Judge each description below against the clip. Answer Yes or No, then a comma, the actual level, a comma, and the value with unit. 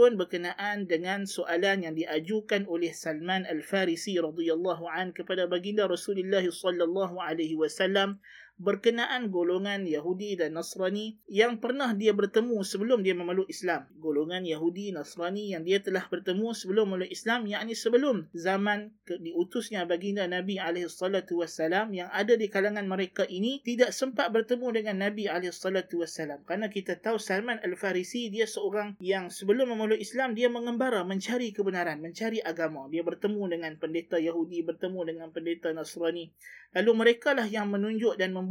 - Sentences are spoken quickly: No, average, 145 wpm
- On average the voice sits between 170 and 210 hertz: Yes, high, 190 Hz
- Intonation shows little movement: No, average, 3.6 semitones